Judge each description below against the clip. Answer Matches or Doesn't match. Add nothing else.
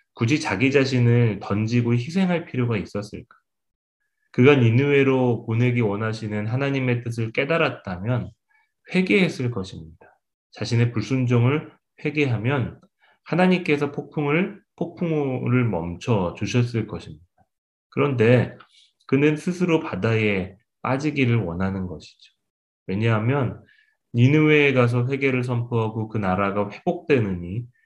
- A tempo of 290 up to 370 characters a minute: Doesn't match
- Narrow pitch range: Doesn't match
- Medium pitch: Doesn't match